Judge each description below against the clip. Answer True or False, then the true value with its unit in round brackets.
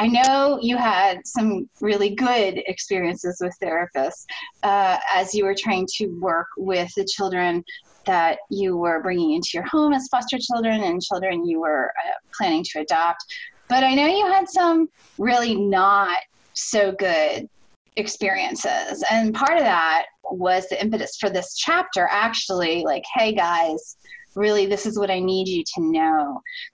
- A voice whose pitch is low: False (200 Hz)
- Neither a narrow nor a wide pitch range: False (6.0 semitones)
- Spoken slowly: False (160 wpm)